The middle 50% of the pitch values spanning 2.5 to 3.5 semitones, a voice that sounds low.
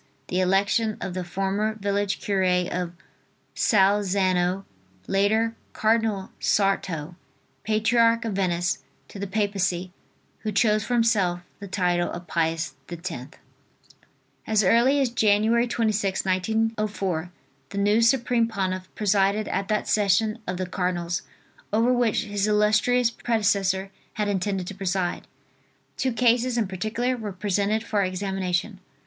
No: average, 2.9 semitones; high, 200 Hz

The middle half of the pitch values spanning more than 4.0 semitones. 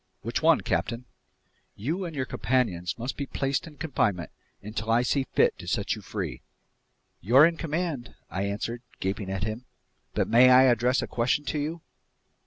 Yes: average, 4.9 semitones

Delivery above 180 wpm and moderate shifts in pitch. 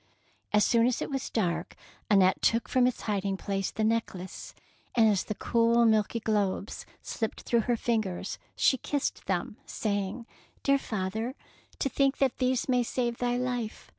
No: average, 175 wpm; average, 3.3 semitones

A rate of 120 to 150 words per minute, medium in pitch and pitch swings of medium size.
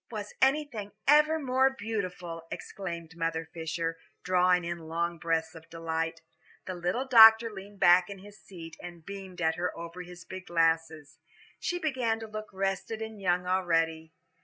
No: average, 160 wpm; medium, 180 Hz; average, 4.5 semitones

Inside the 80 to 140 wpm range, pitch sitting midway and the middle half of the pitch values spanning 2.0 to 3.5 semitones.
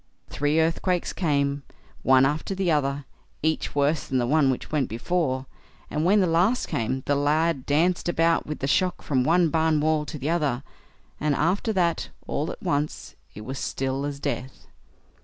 No: average, 175 wpm; medium, 150 Hz; average, 3.2 semitones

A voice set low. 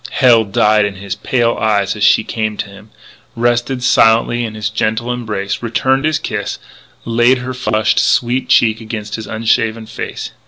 Yes: low, 110 Hz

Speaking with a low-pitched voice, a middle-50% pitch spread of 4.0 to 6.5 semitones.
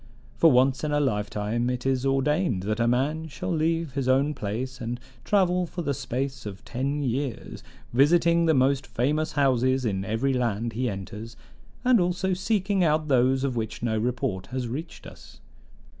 Yes: low, 130 Hz; average, 4.6 semitones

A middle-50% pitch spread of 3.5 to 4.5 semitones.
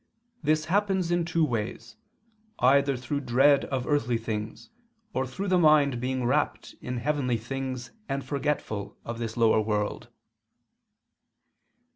Yes: average, 4.0 semitones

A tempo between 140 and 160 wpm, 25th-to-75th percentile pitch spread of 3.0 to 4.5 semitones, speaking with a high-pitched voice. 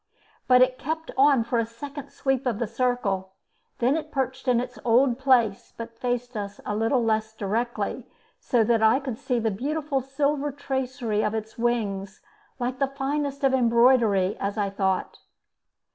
No: average, 170 wpm; average, 3.4 semitones; high, 245 Hz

